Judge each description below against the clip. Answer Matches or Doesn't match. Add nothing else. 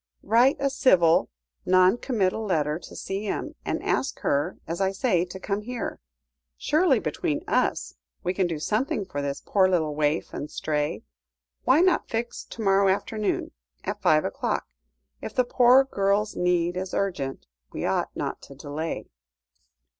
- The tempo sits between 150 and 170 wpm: Matches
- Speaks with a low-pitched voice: Doesn't match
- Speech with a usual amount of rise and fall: Doesn't match